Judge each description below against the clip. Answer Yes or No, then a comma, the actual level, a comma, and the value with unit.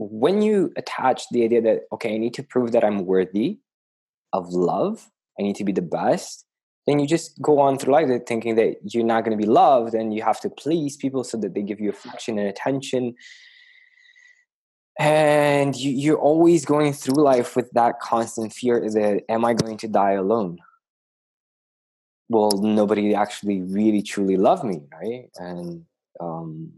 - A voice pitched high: No, low, 115 Hz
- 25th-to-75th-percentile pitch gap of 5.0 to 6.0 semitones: Yes, wide, 5.4 semitones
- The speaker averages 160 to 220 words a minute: Yes, average, 175 wpm